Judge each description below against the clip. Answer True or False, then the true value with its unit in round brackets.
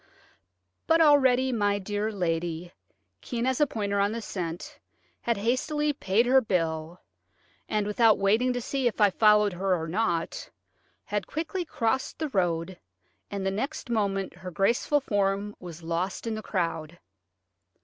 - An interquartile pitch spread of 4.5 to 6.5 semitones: True (4.8 semitones)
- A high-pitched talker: True (205 Hz)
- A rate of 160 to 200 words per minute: False (150 wpm)